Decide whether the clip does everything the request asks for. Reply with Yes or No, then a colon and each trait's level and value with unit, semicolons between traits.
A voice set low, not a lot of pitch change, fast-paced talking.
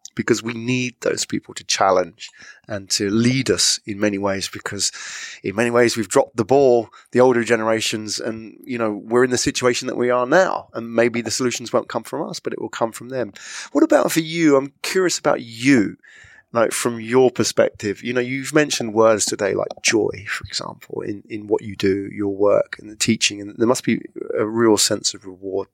No: low, 115 Hz; average, 3.1 semitones; fast, 210 wpm